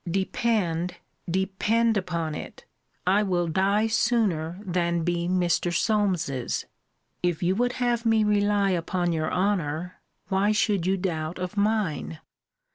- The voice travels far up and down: No, average, 3.3 semitones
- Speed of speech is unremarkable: No, slow, 125 wpm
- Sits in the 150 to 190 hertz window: Yes, medium, 185 Hz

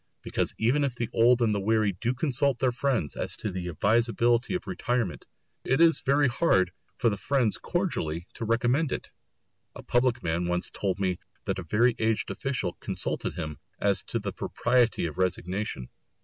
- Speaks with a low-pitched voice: Yes, low, 115 Hz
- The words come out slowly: No, average, 175 wpm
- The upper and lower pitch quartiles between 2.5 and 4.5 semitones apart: No, average, 5.2 semitones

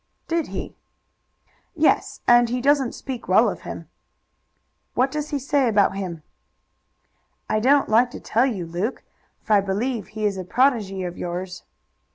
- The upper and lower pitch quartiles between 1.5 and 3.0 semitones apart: No, wide, 5.5 semitones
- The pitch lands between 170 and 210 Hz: No, high, 230 Hz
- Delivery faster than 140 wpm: Yes, average, 160 wpm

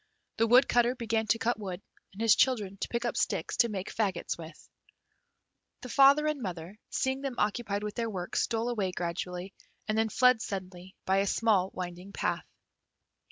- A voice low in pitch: No, high, 215 Hz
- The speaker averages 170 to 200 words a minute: Yes, average, 175 wpm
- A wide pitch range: No, average, 4.2 semitones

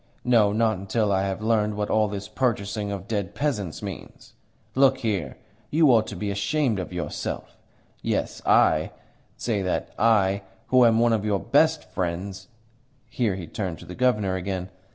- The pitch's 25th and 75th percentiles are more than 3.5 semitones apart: No, average, 3.0 semitones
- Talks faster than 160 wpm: Yes, average, 170 wpm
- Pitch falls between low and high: No, low, 105 Hz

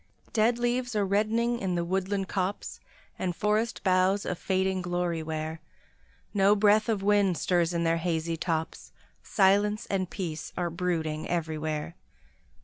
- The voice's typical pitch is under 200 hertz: Yes, medium, 185 Hz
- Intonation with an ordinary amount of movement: Yes, average, 3.5 semitones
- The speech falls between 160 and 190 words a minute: No, average, 145 wpm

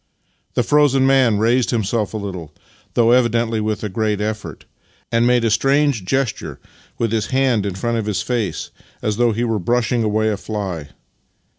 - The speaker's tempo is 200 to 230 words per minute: No, average, 185 wpm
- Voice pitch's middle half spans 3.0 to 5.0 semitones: No, narrow, 2.6 semitones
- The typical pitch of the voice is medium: No, low, 115 Hz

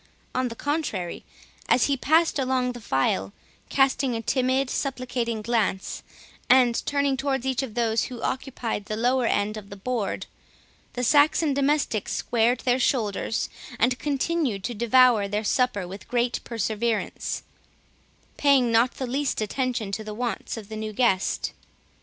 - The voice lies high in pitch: Yes, high, 245 Hz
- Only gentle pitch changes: No, average, 3.4 semitones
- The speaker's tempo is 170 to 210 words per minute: No, average, 150 wpm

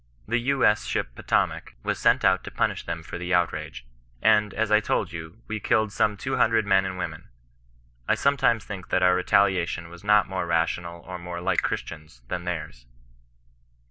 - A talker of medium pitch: No, very low, 95 Hz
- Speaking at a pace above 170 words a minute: Yes, average, 185 wpm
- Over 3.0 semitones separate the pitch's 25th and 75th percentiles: Yes, average, 3.6 semitones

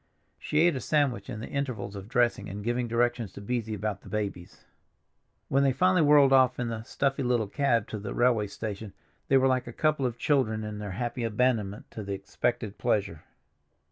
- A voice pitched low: Yes, low, 120 Hz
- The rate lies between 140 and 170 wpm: No, average, 200 wpm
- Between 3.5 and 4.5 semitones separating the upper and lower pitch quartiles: Yes, average, 3.9 semitones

